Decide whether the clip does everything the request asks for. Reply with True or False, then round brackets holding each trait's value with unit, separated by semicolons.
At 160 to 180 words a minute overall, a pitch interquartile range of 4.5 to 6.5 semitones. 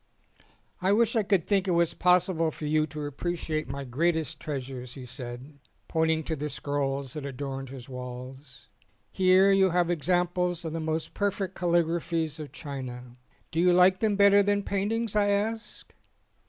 True (165 wpm; 4.9 semitones)